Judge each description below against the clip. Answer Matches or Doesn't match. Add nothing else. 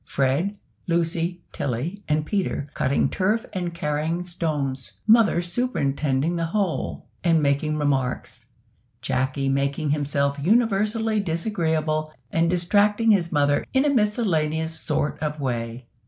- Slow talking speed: Matches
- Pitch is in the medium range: Matches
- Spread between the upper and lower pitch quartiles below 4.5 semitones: Doesn't match